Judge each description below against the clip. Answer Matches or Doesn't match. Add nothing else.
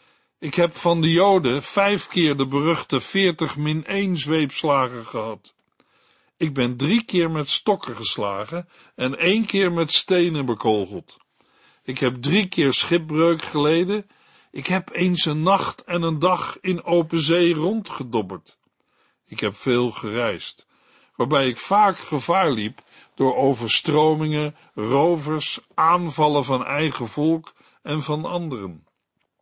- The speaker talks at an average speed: Doesn't match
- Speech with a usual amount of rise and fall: Matches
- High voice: Doesn't match